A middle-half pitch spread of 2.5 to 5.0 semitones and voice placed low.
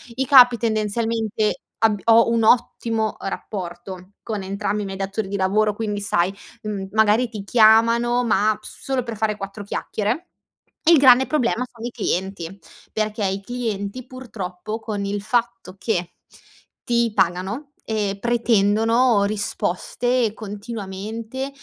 No: average, 2.8 semitones; high, 220 Hz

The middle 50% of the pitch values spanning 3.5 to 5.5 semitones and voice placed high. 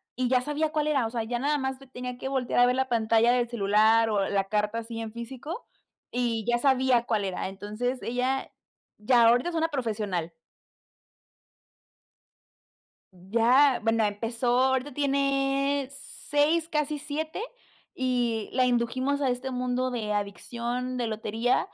No: average, 3.1 semitones; high, 245 Hz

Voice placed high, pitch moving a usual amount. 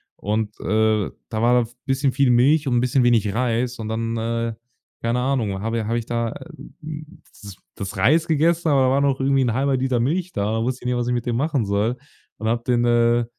No: low, 120 Hz; average, 3.0 semitones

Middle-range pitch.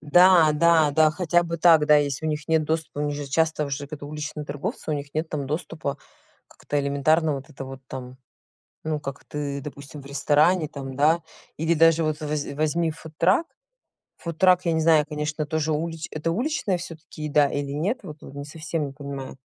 Yes: medium, 150 Hz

